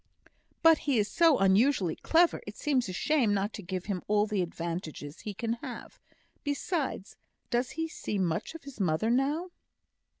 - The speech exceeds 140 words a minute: Yes, average, 170 wpm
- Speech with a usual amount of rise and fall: No, wide, 7.2 semitones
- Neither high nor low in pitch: No, high, 220 Hz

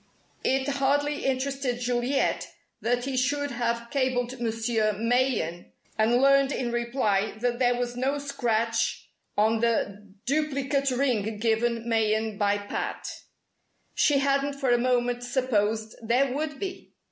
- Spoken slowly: Yes, slow, 130 wpm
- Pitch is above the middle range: Yes, high, 245 Hz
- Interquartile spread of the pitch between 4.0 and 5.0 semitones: No, average, 3.3 semitones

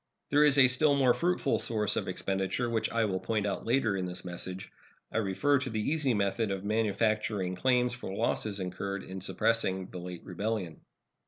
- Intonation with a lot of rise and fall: No, average, 4.4 semitones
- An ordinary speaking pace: Yes, average, 185 wpm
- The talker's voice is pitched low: Yes, low, 105 Hz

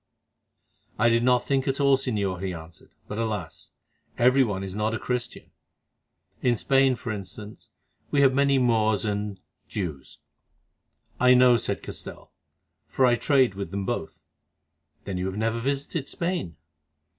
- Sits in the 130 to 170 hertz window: No, low, 115 Hz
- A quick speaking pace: No, average, 145 wpm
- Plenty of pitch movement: No, average, 4.6 semitones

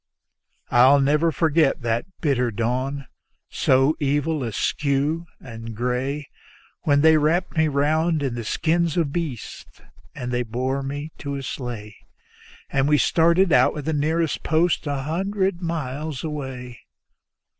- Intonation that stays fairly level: No, average, 3.7 semitones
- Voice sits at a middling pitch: Yes, medium, 145 Hz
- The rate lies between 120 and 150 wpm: Yes, slow, 135 wpm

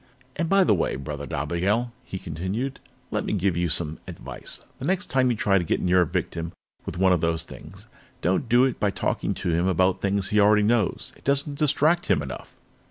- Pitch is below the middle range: Yes, very low, 95 Hz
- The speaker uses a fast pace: Yes, fast, 215 wpm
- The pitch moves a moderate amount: No, wide, 6.1 semitones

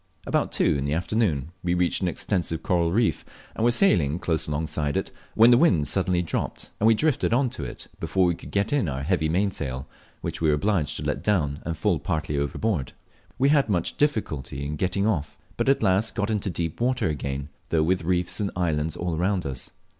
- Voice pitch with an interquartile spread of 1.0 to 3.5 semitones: No, wide, 5.4 semitones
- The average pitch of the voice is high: No, very low, 90 Hz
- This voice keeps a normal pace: No, fast, 215 wpm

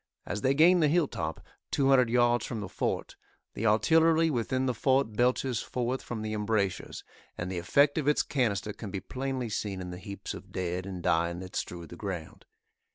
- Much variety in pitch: Yes, wide, 6.0 semitones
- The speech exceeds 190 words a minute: Yes, average, 200 wpm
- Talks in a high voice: No, low, 110 Hz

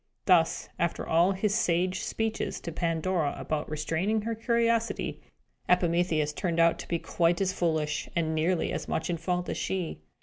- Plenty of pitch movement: No, average, 2.7 semitones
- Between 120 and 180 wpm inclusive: Yes, average, 165 wpm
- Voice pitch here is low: No, medium, 175 Hz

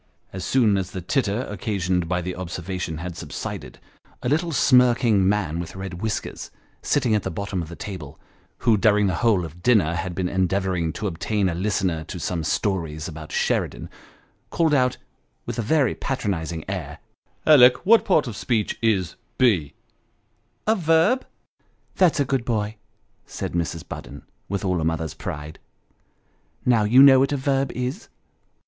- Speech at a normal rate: Yes, average, 170 wpm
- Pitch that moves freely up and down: Yes, wide, 6.2 semitones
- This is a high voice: No, low, 100 Hz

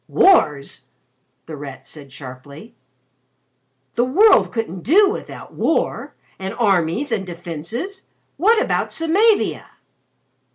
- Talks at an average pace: No, slow, 100 wpm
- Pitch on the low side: No, high, 215 Hz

